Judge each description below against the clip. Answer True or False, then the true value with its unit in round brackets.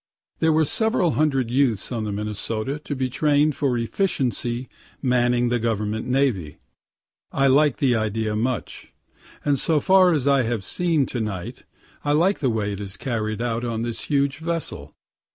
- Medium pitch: False (125 Hz)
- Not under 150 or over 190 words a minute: True (170 wpm)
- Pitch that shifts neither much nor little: True (4.6 semitones)